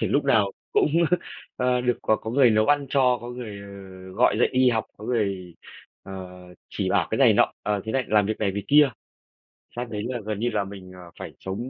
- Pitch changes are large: No, average, 3.9 semitones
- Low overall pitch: Yes, low, 110 Hz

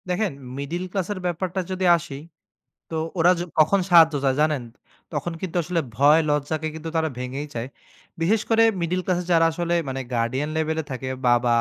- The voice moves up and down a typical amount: Yes, average, 4.0 semitones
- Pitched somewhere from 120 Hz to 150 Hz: No, medium, 160 Hz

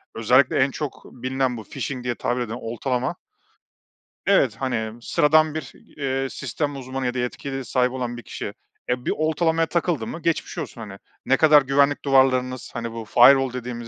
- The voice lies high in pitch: No, low, 130 Hz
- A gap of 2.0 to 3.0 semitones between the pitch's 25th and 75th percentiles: Yes, narrow, 2.5 semitones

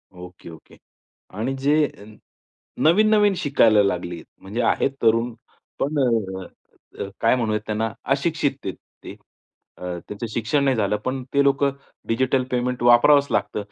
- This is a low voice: Yes, low, 120 Hz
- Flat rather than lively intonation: No, average, 4.8 semitones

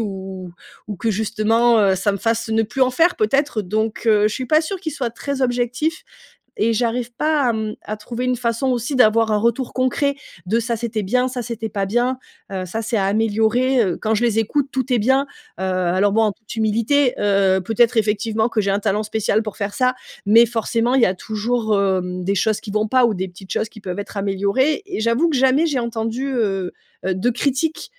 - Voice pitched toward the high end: Yes, high, 225 Hz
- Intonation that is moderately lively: Yes, average, 3.3 semitones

